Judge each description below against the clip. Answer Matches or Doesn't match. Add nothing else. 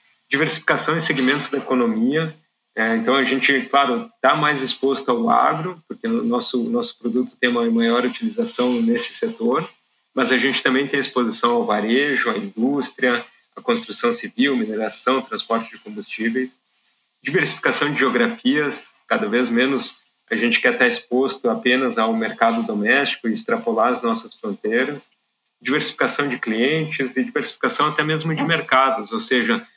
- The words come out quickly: Doesn't match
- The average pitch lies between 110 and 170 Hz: Matches